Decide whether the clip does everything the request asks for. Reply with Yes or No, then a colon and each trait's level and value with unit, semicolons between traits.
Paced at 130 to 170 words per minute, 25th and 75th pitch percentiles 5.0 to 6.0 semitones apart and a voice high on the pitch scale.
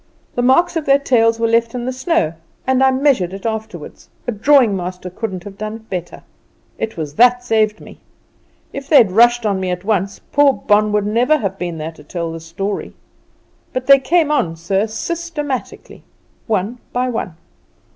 No: average, 185 wpm; wide, 5.4 semitones; high, 225 Hz